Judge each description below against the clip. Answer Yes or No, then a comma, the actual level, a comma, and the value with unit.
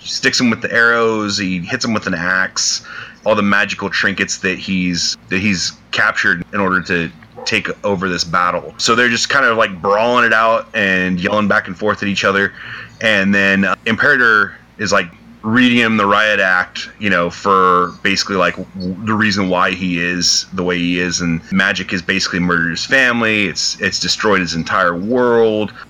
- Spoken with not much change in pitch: No, average, 3.0 semitones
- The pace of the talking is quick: No, average, 190 wpm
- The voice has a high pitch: No, very low, 95 Hz